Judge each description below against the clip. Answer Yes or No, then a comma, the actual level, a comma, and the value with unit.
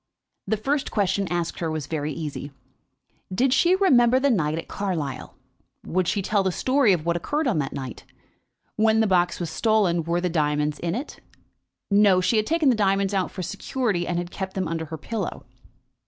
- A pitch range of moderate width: Yes, average, 4.8 semitones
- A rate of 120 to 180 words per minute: No, average, 195 wpm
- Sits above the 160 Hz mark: Yes, medium, 185 Hz